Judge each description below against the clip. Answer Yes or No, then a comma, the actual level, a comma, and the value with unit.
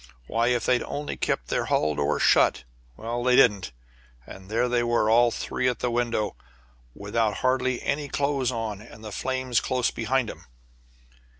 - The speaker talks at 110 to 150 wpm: No, average, 170 wpm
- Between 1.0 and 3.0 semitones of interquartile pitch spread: Yes, average, 2.7 semitones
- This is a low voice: Yes, low, 120 Hz